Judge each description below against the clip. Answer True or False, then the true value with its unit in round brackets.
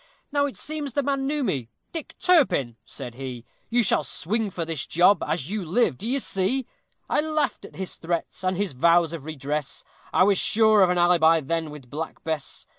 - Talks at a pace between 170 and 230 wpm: True (195 wpm)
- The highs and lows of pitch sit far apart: True (7.3 semitones)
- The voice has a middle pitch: True (180 Hz)